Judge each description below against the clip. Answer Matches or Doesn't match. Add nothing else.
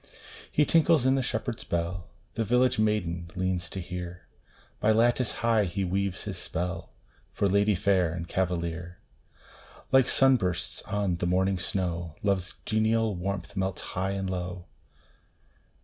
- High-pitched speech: Doesn't match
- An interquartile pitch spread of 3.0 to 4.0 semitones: Matches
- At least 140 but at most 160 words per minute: Matches